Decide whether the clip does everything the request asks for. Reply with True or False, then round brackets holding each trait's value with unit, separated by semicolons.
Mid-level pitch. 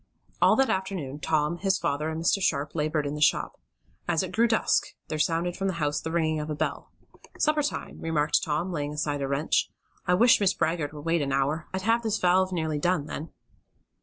True (160 Hz)